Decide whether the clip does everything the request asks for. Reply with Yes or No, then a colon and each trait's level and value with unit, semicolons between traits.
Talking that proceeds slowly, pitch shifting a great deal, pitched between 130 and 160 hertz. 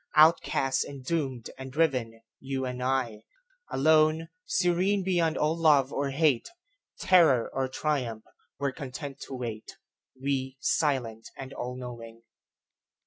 No: slow, 110 wpm; average, 3.9 semitones; low, 135 Hz